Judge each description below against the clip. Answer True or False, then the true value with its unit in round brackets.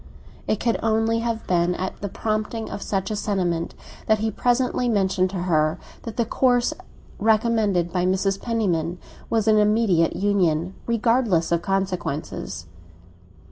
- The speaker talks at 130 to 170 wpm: True (140 wpm)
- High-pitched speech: True (205 Hz)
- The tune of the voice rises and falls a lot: False (4.0 semitones)